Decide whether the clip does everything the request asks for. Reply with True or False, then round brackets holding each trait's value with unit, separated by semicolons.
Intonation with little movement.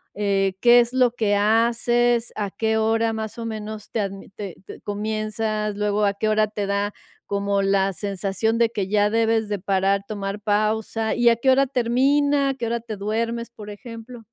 True (2.3 semitones)